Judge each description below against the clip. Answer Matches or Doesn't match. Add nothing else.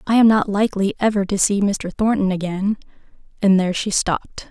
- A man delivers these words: Doesn't match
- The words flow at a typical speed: Matches